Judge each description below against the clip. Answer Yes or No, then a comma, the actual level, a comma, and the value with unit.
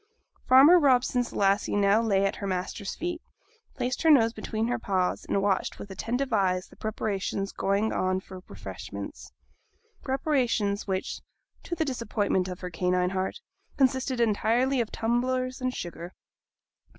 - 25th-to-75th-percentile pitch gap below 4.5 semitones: No, average, 4.8 semitones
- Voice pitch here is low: No, high, 220 Hz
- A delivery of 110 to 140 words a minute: No, average, 150 wpm